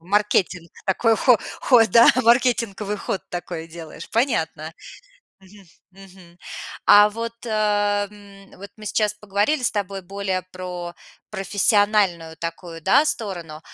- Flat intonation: No, average, 3.0 semitones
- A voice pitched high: Yes, high, 200 Hz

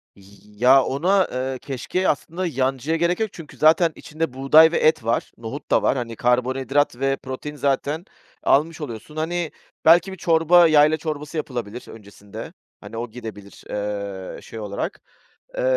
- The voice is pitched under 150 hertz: Yes, low, 135 Hz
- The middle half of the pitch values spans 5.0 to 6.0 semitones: Yes, wide, 5.4 semitones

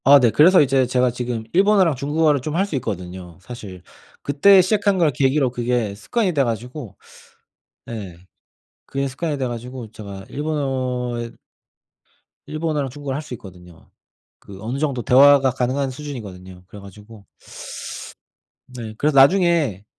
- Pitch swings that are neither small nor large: Yes, average, 4.9 semitones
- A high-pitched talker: No, low, 130 Hz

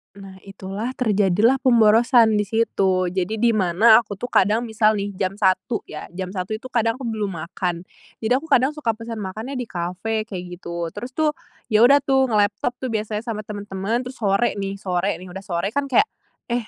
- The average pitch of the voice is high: Yes, high, 215 Hz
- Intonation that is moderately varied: Yes, average, 3.6 semitones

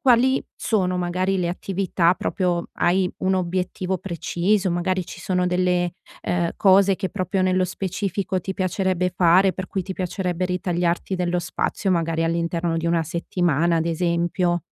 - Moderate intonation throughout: No, narrow, 1.6 semitones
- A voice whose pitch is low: No, medium, 180 Hz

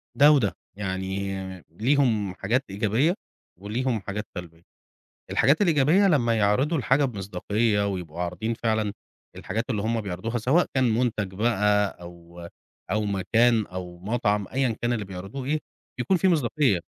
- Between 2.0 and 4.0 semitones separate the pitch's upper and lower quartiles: No, average, 4.5 semitones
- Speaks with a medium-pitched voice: No, low, 110 Hz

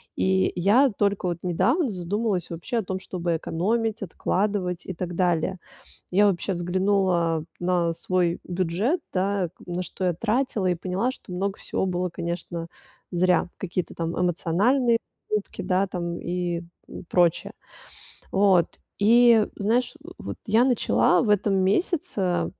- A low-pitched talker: No, medium, 185 Hz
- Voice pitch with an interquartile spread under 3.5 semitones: Yes, average, 2.9 semitones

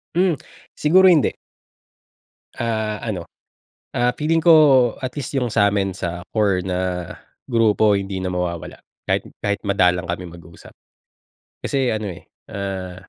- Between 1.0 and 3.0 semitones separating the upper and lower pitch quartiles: No, average, 5.2 semitones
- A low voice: Yes, low, 100 Hz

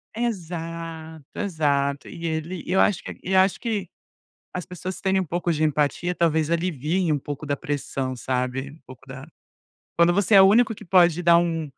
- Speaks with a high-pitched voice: No, medium, 165 Hz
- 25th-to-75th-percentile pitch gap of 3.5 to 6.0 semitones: Yes, average, 3.8 semitones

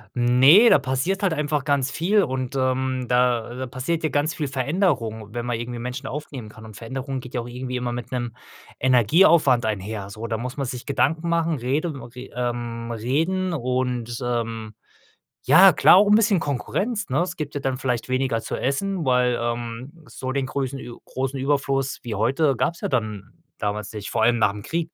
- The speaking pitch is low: Yes, low, 130 Hz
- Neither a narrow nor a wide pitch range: Yes, average, 3.5 semitones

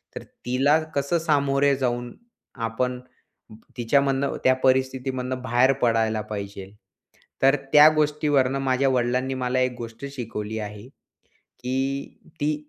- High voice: No, low, 130 Hz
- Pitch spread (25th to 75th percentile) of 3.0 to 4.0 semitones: No, narrow, 2.4 semitones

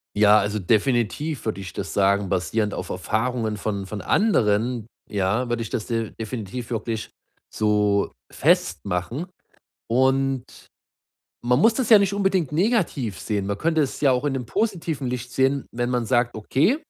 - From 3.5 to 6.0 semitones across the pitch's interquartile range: Yes, average, 4.7 semitones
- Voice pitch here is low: Yes, low, 120 Hz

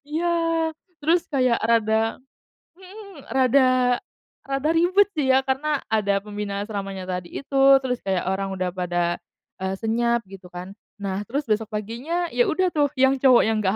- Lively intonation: Yes, wide, 5.9 semitones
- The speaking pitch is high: Yes, high, 230 Hz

